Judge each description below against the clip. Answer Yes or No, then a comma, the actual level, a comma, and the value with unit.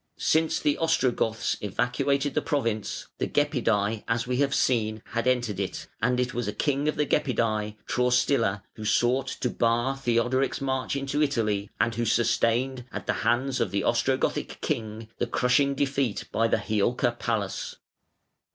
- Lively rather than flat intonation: No, average, 3.3 semitones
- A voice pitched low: Yes, low, 120 Hz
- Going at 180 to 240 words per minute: No, average, 165 wpm